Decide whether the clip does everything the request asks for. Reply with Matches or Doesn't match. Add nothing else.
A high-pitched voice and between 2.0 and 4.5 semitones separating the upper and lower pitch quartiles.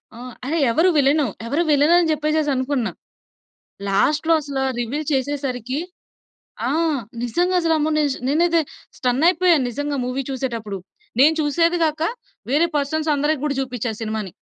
Matches